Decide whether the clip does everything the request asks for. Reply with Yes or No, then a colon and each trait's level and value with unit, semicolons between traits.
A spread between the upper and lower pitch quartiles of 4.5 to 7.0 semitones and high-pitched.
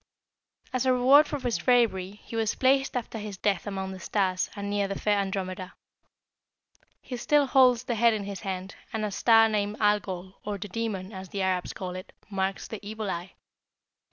No: average, 3.2 semitones; high, 205 Hz